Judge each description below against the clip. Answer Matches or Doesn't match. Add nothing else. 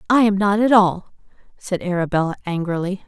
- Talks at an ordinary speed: Matches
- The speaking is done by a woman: Matches